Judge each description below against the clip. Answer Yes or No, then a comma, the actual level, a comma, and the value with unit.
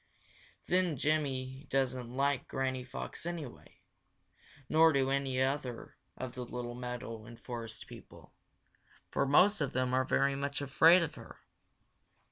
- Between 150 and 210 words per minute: No, slow, 135 wpm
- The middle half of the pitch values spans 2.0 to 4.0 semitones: Yes, narrow, 2.4 semitones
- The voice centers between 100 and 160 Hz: Yes, low, 135 Hz